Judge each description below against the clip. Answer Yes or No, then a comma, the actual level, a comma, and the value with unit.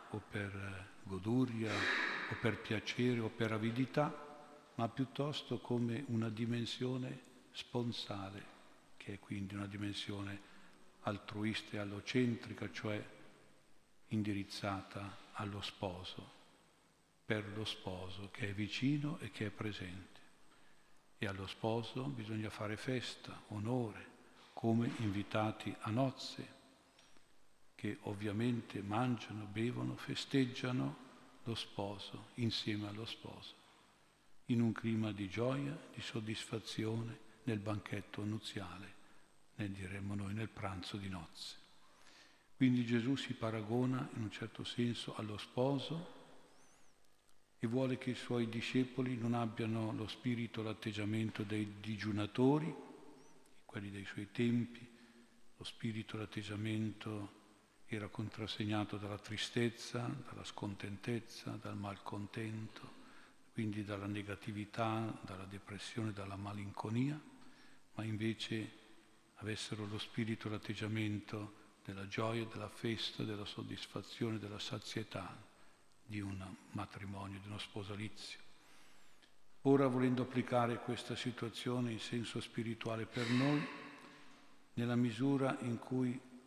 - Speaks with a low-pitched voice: Yes, low, 110 Hz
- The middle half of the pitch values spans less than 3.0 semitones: Yes, narrow, 2.6 semitones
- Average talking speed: No, slow, 105 wpm